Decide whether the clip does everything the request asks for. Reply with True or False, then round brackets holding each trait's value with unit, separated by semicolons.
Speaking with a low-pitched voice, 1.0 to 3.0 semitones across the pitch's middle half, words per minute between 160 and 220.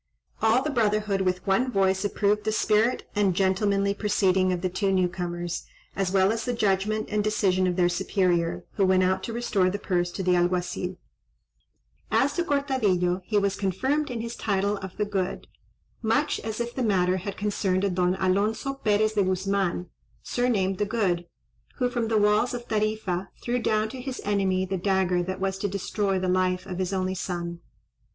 False (195 Hz; 2.6 semitones; 190 wpm)